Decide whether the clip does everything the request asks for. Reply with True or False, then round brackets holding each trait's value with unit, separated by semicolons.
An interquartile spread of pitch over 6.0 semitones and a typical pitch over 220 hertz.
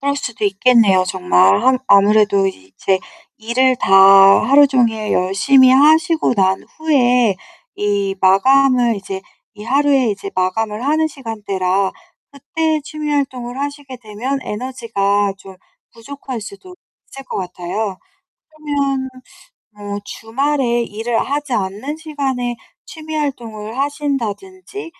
False (5.6 semitones; 240 Hz)